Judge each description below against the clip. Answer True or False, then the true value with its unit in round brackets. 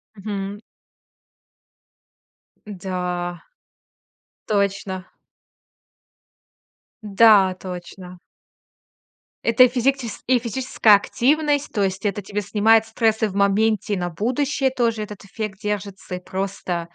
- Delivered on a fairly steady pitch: False (3.0 semitones)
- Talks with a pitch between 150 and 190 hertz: False (205 Hz)